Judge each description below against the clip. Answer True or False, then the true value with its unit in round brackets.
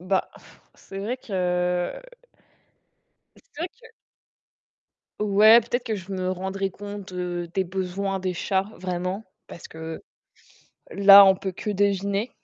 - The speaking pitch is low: False (195 Hz)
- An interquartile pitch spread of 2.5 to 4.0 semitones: False (1.9 semitones)